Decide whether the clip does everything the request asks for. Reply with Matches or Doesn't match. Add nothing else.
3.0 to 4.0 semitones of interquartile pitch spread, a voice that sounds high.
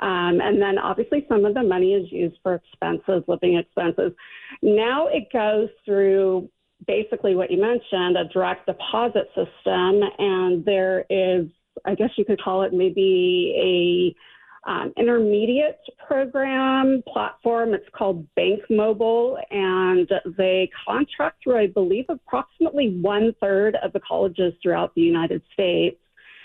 Doesn't match